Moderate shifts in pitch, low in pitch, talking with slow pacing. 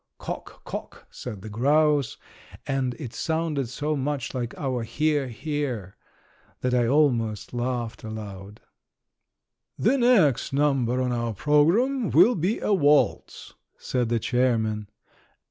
Yes: average, 4.4 semitones; low, 130 Hz; slow, 125 wpm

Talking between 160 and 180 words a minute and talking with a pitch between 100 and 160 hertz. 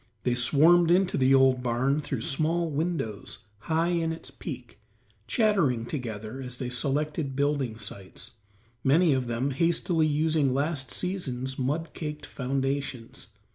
No: slow, 135 wpm; medium, 140 Hz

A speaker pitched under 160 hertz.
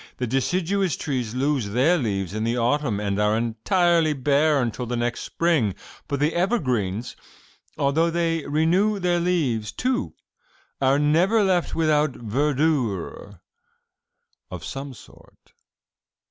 Yes: medium, 140 Hz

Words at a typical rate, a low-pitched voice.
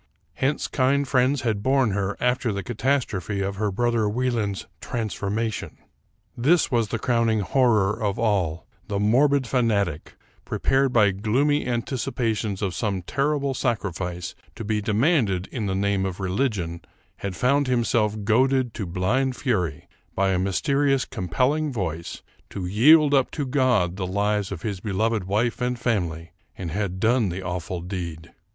Yes: average, 155 wpm; low, 110 Hz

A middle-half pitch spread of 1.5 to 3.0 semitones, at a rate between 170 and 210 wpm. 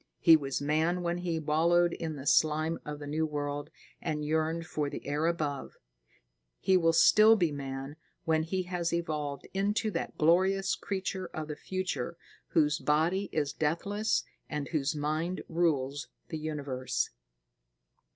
No: average, 2.7 semitones; average, 150 wpm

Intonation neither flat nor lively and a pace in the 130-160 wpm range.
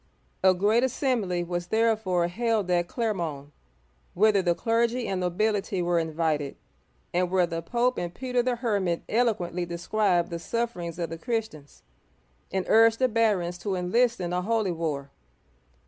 Yes: average, 4.7 semitones; average, 150 wpm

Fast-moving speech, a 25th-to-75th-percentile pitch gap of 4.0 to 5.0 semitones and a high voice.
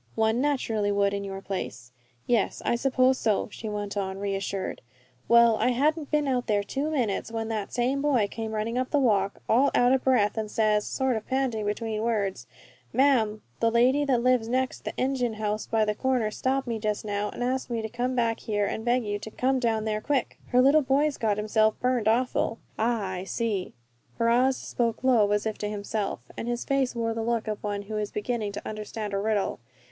No: fast, 210 wpm; average, 3.3 semitones; high, 225 Hz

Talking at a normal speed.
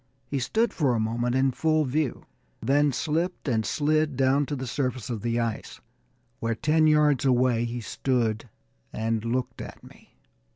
Yes: average, 165 wpm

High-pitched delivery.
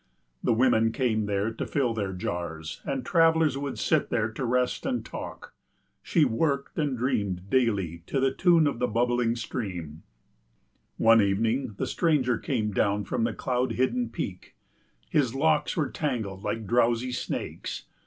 No: low, 120 Hz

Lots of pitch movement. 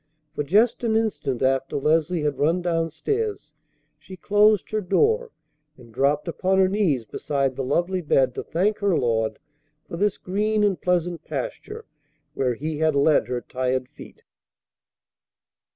Yes: wide, 7.1 semitones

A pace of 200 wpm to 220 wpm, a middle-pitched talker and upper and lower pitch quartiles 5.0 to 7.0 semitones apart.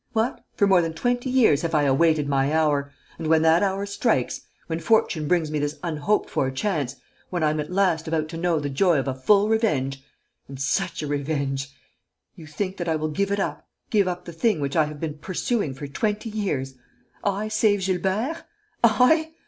Yes: fast, 205 wpm; medium, 165 Hz; wide, 5.4 semitones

